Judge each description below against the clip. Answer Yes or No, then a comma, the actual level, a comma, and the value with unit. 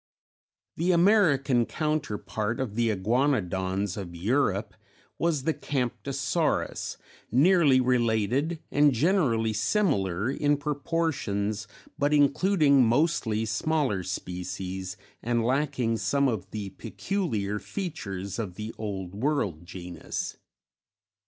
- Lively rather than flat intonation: Yes, wide, 6.5 semitones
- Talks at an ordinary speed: No, slow, 100 wpm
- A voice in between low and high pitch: No, low, 120 Hz